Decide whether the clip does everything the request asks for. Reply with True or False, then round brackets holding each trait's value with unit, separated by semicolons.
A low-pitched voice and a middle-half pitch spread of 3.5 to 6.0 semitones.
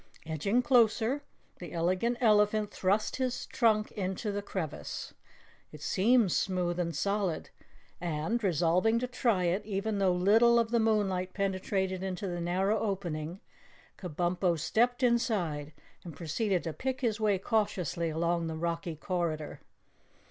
False (190 Hz; 4.2 semitones)